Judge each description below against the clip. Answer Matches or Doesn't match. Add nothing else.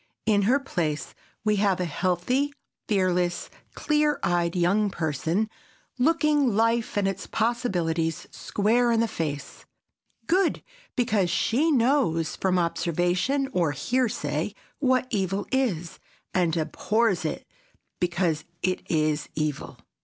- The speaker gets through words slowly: Matches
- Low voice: Doesn't match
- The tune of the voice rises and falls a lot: Matches